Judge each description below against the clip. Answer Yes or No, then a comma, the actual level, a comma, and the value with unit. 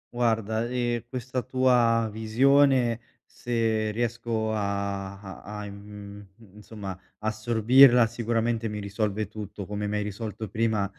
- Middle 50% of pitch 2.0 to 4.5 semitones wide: Yes, narrow, 2.4 semitones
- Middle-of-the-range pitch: No, low, 110 Hz